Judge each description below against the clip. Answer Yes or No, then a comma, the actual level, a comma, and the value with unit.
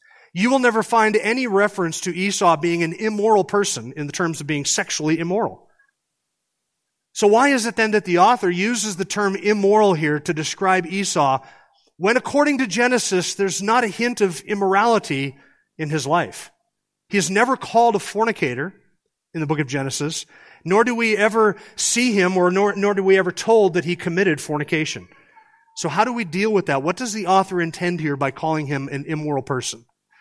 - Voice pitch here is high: Yes, high, 195 Hz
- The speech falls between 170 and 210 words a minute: Yes, average, 190 wpm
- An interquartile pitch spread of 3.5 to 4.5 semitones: No, wide, 5.4 semitones